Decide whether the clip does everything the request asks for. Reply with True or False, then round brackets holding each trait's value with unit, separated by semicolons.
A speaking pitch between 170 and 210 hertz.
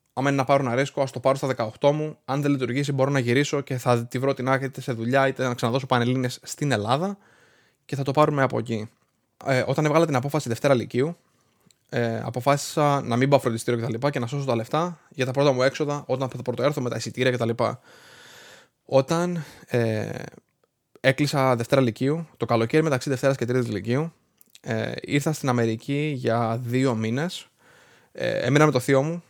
False (135 Hz)